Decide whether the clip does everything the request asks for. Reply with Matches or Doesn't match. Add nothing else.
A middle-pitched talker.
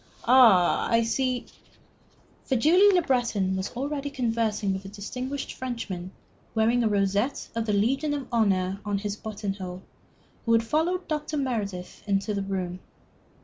Doesn't match